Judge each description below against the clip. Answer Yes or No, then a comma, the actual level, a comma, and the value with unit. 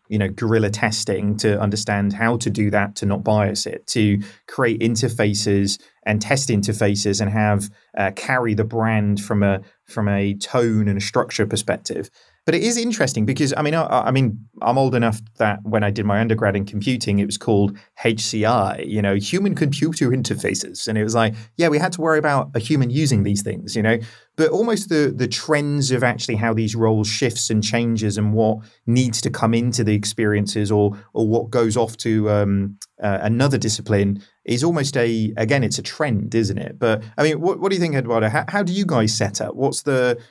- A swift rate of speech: Yes, fast, 210 wpm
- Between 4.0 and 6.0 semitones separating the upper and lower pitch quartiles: No, average, 3.4 semitones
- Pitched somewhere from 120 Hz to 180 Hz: No, low, 110 Hz